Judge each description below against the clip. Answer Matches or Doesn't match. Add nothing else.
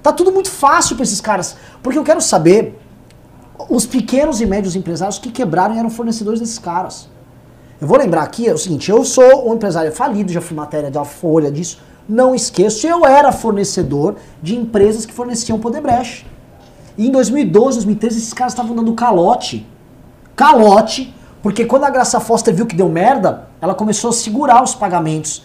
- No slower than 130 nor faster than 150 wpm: Doesn't match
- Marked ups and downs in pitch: Matches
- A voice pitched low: Doesn't match